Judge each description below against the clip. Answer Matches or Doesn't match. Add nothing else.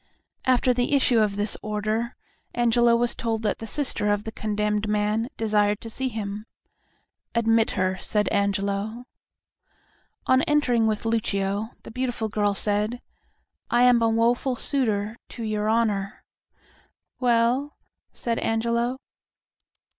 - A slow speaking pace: Matches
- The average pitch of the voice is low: Doesn't match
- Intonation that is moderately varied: Doesn't match